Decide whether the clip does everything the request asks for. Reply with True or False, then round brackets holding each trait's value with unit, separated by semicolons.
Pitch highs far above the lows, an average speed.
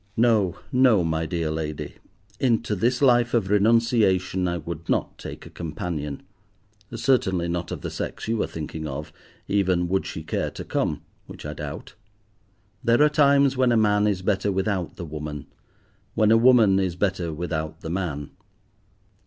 True (5.8 semitones; 165 wpm)